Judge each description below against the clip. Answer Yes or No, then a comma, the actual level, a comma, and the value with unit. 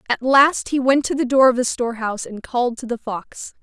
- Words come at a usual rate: No, fast, 250 wpm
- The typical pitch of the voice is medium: No, very high, 250 Hz